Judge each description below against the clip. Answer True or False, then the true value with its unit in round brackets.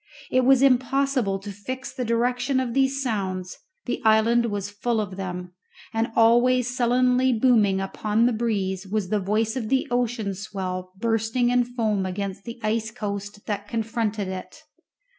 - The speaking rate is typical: True (160 wpm)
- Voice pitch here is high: True (225 Hz)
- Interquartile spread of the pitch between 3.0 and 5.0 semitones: True (3.5 semitones)